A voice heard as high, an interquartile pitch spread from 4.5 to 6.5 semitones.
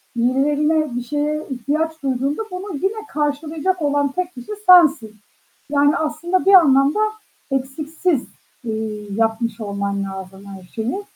Yes: very high, 285 Hz; average, 5.1 semitones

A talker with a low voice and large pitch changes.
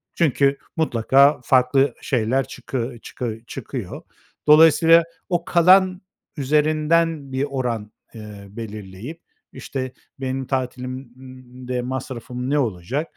No: low, 130 Hz; average, 3.4 semitones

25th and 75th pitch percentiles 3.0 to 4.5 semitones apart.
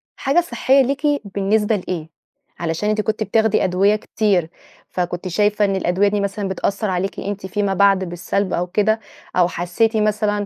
No: narrow, 2.5 semitones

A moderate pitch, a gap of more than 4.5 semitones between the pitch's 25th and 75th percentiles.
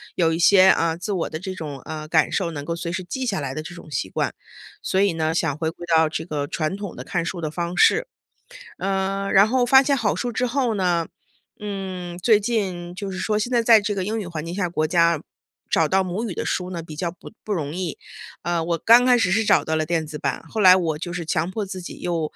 No: medium, 180 Hz; average, 3.7 semitones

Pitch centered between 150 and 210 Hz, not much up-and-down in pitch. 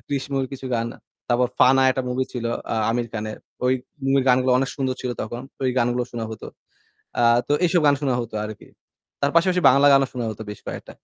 No: low, 130 Hz; narrow, 2.2 semitones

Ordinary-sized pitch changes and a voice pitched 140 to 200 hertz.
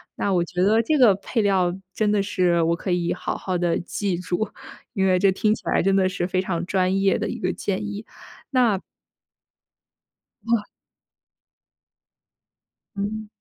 No: narrow, 2.3 semitones; high, 190 Hz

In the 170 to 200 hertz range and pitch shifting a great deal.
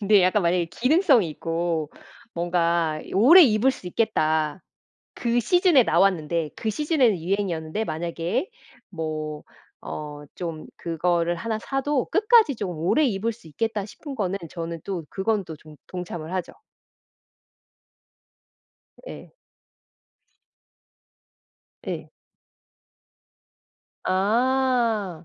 Yes: medium, 185 Hz; wide, 5.8 semitones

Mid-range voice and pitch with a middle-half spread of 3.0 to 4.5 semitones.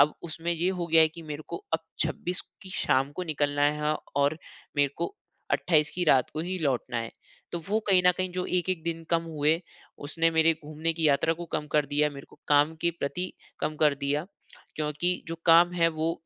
No: medium, 160 Hz; narrow, 2.6 semitones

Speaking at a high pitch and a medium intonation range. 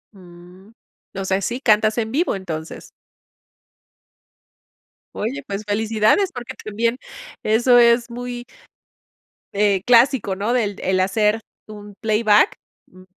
Yes: high, 215 Hz; average, 3.3 semitones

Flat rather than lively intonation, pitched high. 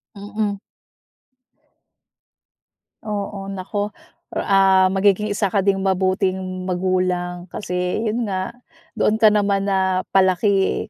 Yes: narrow, 1.5 semitones; high, 195 Hz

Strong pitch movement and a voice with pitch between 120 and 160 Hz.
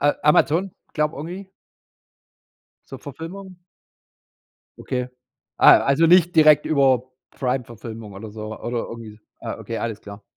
Yes: wide, 6.0 semitones; low, 135 Hz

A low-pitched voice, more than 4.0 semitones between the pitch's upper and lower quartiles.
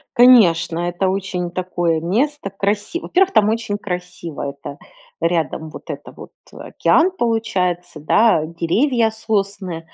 No: high, 190 Hz; average, 4.8 semitones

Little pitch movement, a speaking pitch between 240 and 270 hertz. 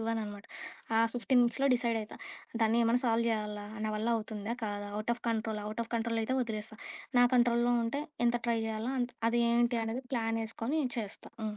No: narrow, 1.7 semitones; high, 230 Hz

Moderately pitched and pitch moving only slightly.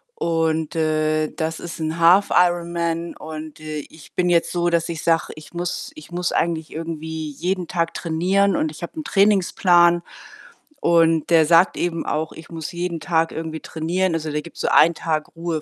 Yes: medium, 165 Hz; narrow, 1.6 semitones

